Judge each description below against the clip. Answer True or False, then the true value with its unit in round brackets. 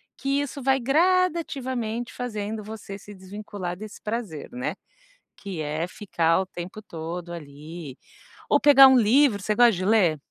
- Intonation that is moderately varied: False (6.0 semitones)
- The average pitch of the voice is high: True (210 Hz)